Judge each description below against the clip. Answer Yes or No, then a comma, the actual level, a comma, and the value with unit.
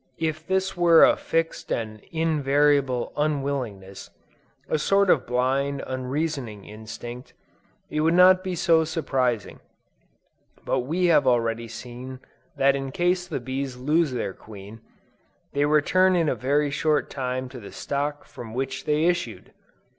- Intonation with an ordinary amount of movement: Yes, average, 4.4 semitones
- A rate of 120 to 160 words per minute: Yes, average, 140 wpm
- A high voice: No, medium, 140 Hz